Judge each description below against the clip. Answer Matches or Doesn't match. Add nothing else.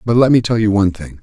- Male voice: Matches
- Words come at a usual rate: Doesn't match